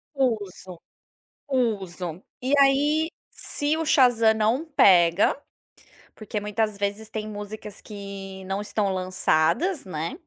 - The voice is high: Yes, high, 210 Hz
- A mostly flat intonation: No, average, 5.0 semitones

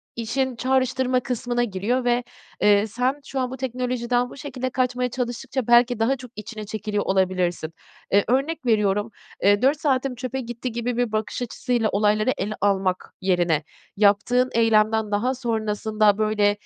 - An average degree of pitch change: Yes, average, 3.2 semitones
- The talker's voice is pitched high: Yes, high, 235 Hz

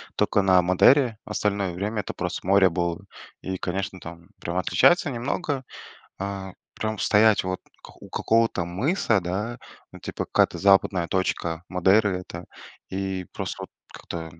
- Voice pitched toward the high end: No, very low, 95 Hz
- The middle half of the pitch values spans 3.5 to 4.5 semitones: No, average, 3.1 semitones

